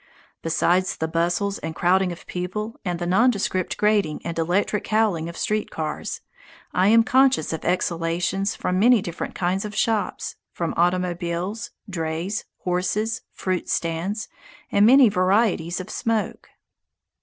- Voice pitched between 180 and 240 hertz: Yes, medium, 185 Hz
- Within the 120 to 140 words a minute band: Yes, slow, 135 wpm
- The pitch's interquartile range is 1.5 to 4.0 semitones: Yes, average, 3.6 semitones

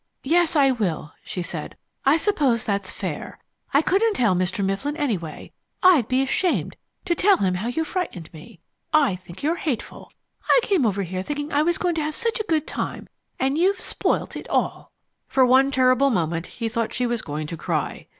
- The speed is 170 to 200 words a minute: Yes, average, 195 wpm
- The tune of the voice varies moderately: No, wide, 8.6 semitones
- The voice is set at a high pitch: Yes, very high, 260 Hz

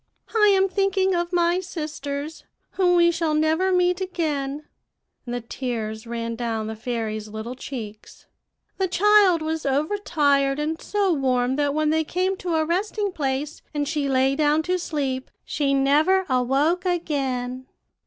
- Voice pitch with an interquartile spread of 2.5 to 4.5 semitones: No, average, 5.2 semitones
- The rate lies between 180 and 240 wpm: No, average, 155 wpm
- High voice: Yes, very high, 300 Hz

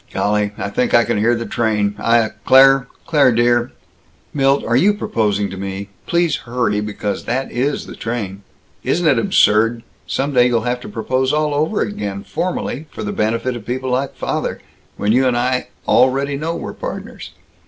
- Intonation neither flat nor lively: Yes, average, 3.9 semitones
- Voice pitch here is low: Yes, low, 120 Hz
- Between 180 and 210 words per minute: Yes, average, 185 wpm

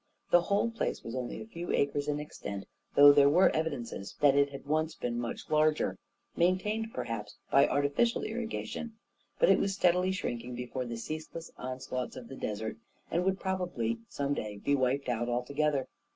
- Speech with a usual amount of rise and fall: No, wide, 6.0 semitones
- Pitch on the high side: No, medium, 145 Hz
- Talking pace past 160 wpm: Yes, average, 180 wpm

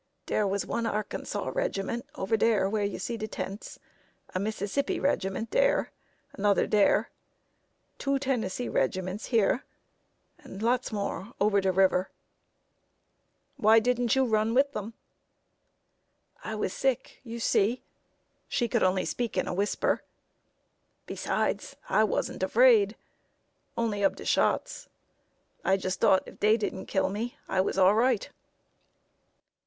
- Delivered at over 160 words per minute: No, slow, 135 wpm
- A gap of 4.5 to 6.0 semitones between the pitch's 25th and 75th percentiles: No, average, 3.7 semitones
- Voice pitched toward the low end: No, high, 215 Hz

